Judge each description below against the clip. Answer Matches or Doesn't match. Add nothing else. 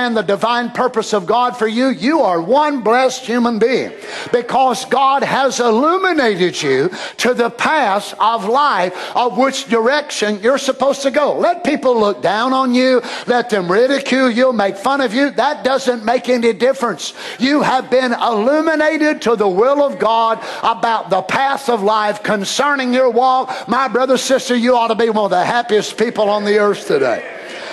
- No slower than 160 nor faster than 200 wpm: Matches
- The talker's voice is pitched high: Matches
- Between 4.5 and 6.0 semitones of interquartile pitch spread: Doesn't match